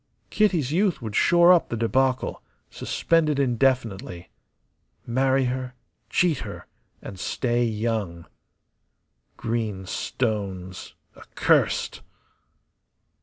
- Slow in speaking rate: Yes, slow, 90 wpm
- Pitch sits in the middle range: No, low, 125 Hz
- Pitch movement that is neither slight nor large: Yes, average, 4.1 semitones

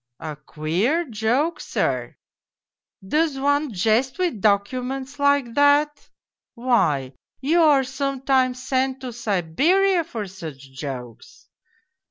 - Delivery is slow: Yes, slow, 110 wpm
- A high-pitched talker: Yes, very high, 255 Hz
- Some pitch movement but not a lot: No, wide, 6.3 semitones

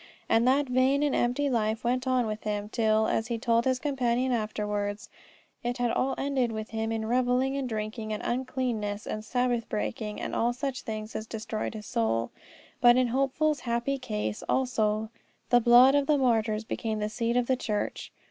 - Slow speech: No, average, 185 wpm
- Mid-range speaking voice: No, high, 235 Hz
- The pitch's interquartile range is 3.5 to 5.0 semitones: No, average, 2.9 semitones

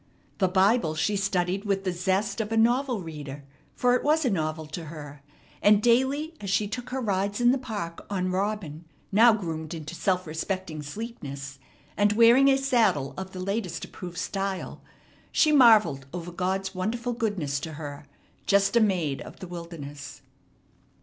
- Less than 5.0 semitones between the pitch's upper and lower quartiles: No, wide, 5.5 semitones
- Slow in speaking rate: No, average, 170 wpm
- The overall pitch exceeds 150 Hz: Yes, high, 190 Hz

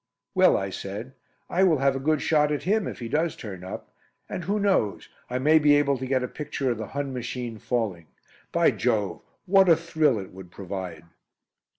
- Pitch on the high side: No, low, 130 Hz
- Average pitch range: No, wide, 6.7 semitones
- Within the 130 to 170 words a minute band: No, fast, 205 wpm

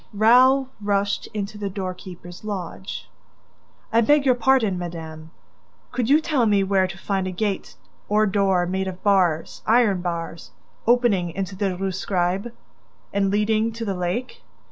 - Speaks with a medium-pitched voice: No, high, 200 Hz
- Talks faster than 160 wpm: No, average, 150 wpm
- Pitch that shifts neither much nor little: Yes, average, 3.4 semitones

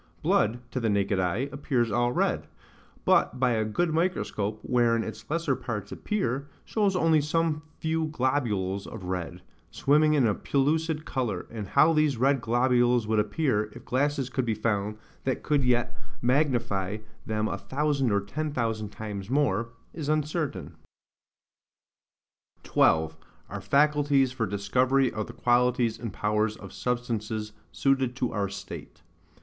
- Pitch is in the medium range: No, low, 120 Hz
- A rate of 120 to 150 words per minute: Yes, average, 145 wpm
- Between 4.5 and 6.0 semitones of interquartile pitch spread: Yes, average, 5.1 semitones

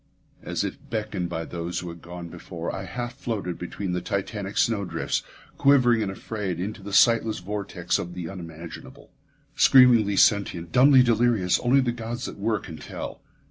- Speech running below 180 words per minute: Yes, average, 165 wpm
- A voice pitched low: Yes, low, 100 Hz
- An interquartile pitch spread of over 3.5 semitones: Yes, average, 4.8 semitones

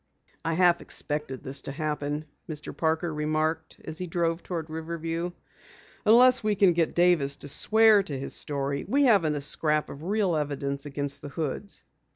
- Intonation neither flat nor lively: Yes, average, 3.3 semitones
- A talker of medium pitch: Yes, medium, 160 Hz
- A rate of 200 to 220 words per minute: No, average, 170 wpm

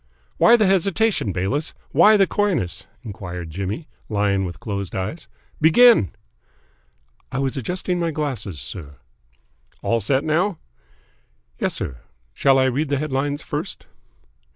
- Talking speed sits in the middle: No, slow, 130 wpm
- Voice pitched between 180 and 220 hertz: No, low, 135 Hz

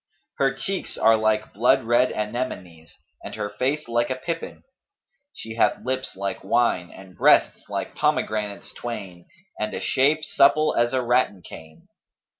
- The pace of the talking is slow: No, average, 150 wpm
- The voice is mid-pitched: No, low, 115 Hz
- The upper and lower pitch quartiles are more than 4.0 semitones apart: Yes, average, 4.4 semitones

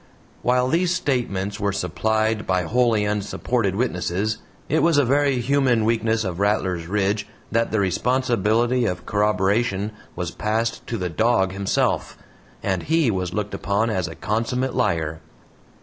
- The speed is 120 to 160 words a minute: Yes, average, 145 wpm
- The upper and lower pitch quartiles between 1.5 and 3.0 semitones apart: No, average, 4.0 semitones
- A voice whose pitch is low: Yes, low, 110 Hz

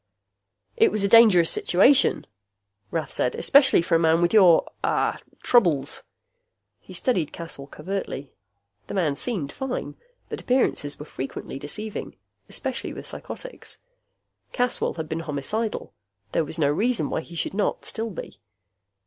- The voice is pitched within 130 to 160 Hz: No, medium, 175 Hz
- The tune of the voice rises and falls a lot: Yes, wide, 6.6 semitones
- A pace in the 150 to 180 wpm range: No, average, 140 wpm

